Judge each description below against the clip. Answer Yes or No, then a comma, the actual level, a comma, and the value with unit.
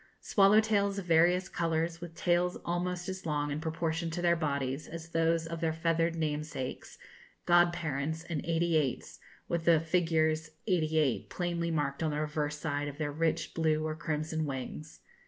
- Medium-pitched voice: Yes, medium, 160 Hz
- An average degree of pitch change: No, narrow, 2.0 semitones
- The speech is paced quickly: No, average, 170 wpm